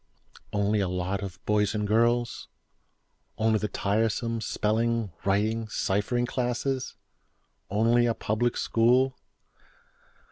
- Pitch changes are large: No, narrow, 2.5 semitones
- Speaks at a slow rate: Yes, slow, 95 wpm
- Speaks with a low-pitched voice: Yes, low, 110 Hz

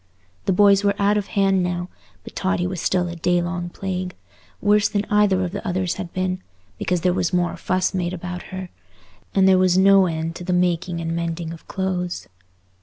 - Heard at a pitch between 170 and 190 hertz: Yes, medium, 185 Hz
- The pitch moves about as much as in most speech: No, narrow, 1.5 semitones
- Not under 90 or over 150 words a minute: No, average, 200 wpm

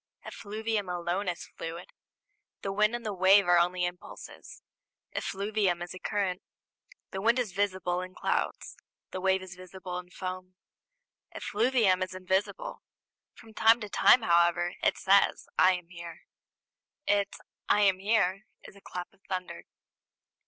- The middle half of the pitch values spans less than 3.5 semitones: Yes, narrow, 2.4 semitones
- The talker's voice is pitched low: No, high, 190 Hz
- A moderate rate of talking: Yes, average, 145 wpm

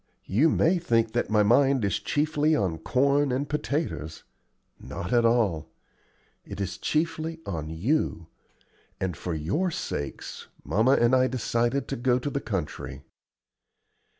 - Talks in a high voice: No, low, 120 Hz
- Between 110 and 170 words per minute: Yes, average, 140 wpm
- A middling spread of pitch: No, wide, 7.1 semitones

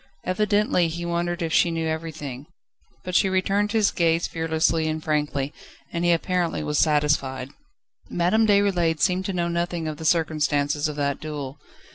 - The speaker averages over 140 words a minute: Yes, average, 160 wpm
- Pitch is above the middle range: No, medium, 165 Hz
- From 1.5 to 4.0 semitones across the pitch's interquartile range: Yes, average, 2.8 semitones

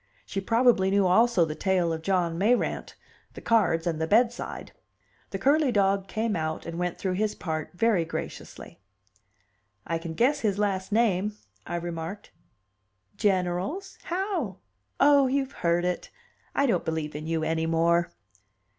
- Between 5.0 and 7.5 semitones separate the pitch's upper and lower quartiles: Yes, average, 5.3 semitones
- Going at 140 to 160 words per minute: Yes, average, 150 wpm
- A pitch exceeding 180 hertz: Yes, high, 190 Hz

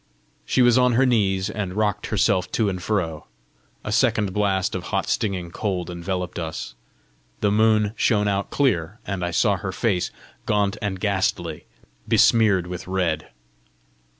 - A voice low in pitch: Yes, low, 100 Hz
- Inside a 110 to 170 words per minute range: Yes, average, 150 wpm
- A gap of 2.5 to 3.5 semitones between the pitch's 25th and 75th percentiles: Yes, average, 2.9 semitones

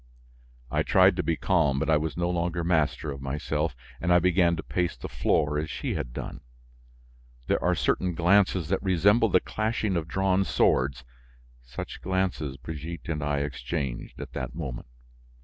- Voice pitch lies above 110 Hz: No, very low, 80 Hz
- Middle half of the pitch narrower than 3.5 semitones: No, average, 4.0 semitones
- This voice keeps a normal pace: Yes, average, 170 wpm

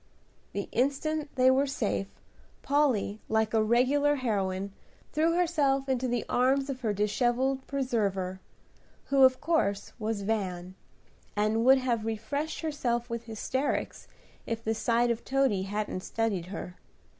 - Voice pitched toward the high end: Yes, high, 235 Hz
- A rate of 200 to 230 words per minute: No, slow, 135 wpm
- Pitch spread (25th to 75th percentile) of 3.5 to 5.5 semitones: Yes, average, 4.4 semitones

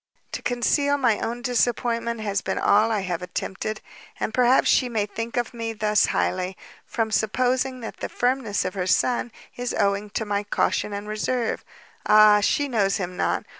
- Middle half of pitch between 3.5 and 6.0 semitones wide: No, average, 3.0 semitones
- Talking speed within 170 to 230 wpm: Yes, average, 175 wpm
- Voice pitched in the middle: No, high, 220 Hz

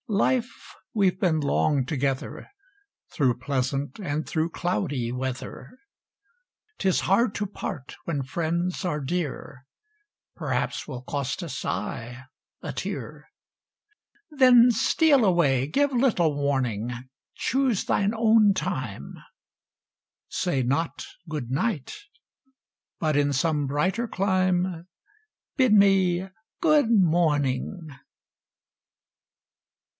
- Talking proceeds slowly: Yes, slow, 100 wpm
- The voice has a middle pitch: Yes, medium, 165 Hz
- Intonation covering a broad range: Yes, wide, 6.6 semitones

